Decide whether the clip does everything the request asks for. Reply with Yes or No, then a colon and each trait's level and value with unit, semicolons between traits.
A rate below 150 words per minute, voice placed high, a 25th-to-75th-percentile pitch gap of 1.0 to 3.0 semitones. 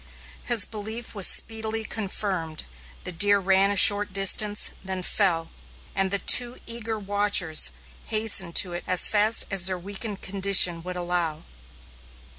Yes: average, 140 wpm; high, 200 Hz; average, 2.7 semitones